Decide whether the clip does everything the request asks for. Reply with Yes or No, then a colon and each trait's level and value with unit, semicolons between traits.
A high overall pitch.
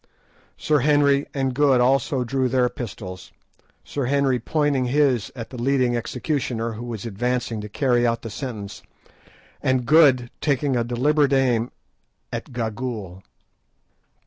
No: low, 125 Hz